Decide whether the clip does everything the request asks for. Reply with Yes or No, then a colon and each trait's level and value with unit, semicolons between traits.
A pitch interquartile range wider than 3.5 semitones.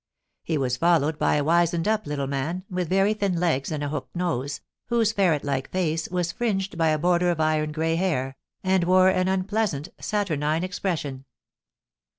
Yes: average, 3.9 semitones